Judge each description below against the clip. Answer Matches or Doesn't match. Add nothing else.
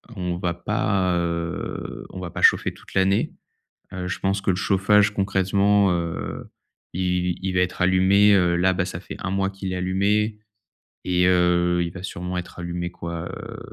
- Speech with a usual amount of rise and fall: Doesn't match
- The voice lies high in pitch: Doesn't match